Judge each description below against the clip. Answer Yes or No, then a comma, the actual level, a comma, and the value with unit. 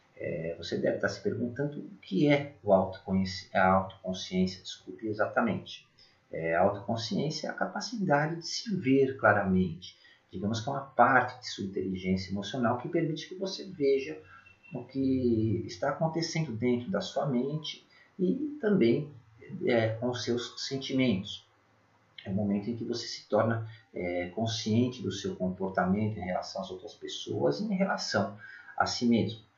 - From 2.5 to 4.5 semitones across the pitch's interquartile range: No, wide, 5.5 semitones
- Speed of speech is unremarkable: Yes, average, 150 wpm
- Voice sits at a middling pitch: No, low, 120 Hz